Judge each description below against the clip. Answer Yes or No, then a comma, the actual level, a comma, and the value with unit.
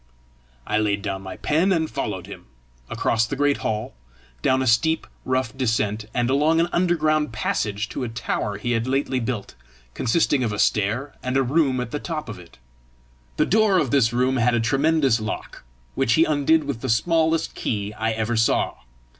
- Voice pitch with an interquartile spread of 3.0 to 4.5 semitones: No, average, 5.1 semitones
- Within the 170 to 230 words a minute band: Yes, average, 190 wpm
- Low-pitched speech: Yes, low, 125 Hz